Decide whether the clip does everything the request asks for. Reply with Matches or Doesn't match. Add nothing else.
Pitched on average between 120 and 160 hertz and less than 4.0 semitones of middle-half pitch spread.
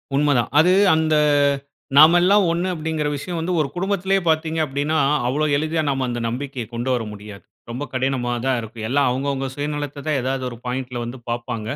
Doesn't match